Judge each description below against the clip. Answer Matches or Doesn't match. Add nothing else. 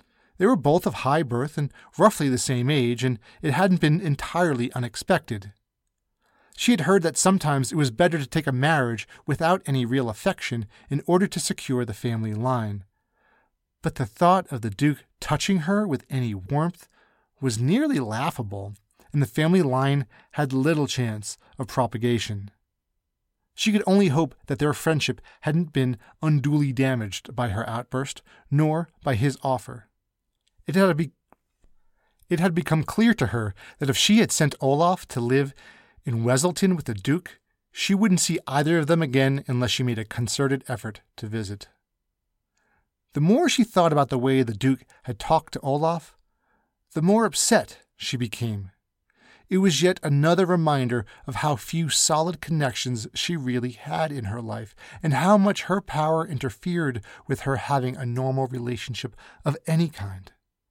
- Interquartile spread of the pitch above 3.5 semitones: Matches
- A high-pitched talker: Doesn't match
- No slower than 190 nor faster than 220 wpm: Doesn't match